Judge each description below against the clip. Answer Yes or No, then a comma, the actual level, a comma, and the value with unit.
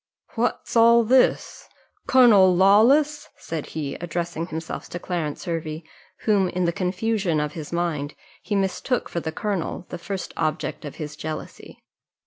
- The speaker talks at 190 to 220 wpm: No, average, 145 wpm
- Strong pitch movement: No, average, 4.9 semitones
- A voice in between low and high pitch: Yes, medium, 175 Hz